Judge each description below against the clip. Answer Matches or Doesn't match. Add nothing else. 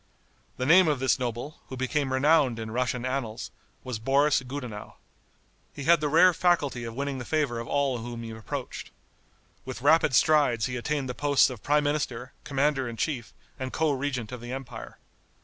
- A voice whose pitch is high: Doesn't match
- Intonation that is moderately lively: Matches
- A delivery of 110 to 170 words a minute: Doesn't match